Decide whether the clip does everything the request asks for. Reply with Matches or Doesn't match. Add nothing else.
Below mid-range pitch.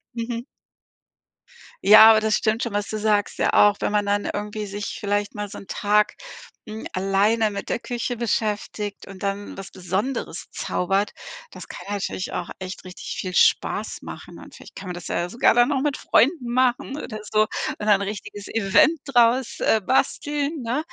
Doesn't match